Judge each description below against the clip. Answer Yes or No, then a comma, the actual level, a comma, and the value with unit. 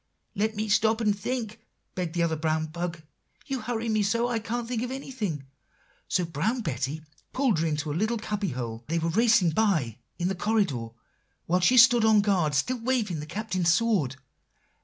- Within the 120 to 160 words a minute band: No, average, 185 wpm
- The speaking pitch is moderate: No, high, 200 Hz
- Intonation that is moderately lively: No, wide, 5.8 semitones